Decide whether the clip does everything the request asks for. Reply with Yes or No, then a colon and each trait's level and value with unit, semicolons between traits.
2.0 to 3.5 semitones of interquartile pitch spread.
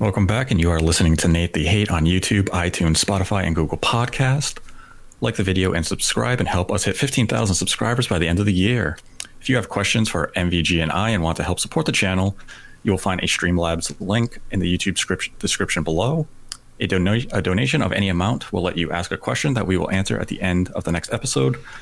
No: average, 4.1 semitones